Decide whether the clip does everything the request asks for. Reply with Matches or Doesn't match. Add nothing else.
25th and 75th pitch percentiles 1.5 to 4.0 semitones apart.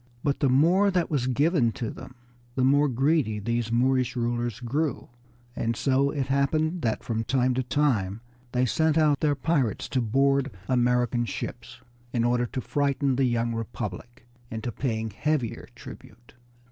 Matches